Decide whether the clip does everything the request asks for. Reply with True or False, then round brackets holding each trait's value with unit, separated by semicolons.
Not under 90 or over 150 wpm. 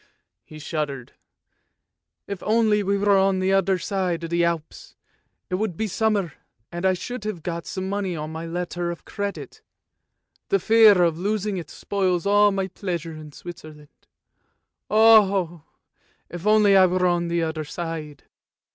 False (160 wpm)